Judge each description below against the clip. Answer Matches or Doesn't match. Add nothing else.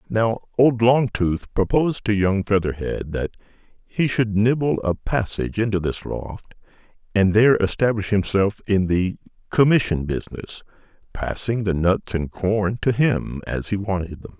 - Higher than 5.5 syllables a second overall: Doesn't match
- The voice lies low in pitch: Matches